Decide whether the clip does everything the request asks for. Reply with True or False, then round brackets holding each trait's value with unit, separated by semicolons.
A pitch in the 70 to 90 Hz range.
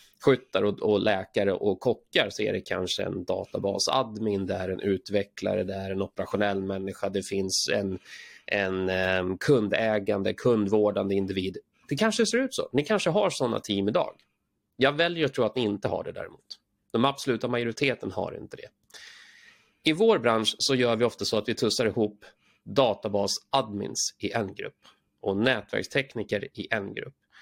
False (105 Hz)